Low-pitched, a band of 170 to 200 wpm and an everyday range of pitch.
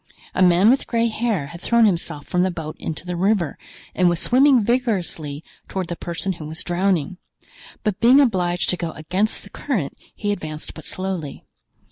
No: medium, 185 Hz; average, 180 wpm; average, 4.3 semitones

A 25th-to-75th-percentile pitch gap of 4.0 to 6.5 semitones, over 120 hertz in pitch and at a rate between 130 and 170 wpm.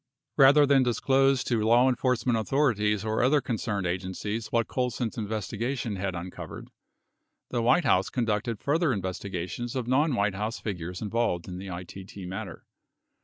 No: average, 4.4 semitones; low, 110 Hz; average, 155 wpm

